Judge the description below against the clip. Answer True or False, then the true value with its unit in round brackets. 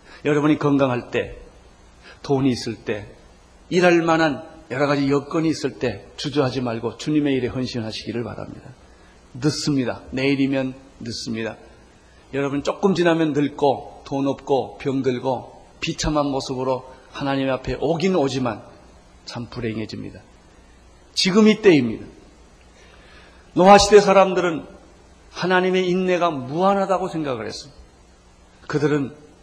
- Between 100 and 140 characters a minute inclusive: False (280 characters per minute)